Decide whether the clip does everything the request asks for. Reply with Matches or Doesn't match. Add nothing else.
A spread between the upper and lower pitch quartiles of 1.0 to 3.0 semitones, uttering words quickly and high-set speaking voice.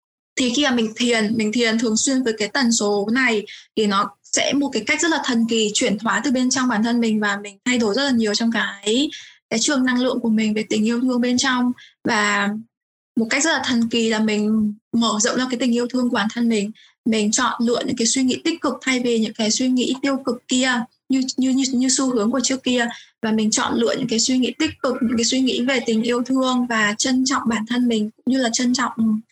Matches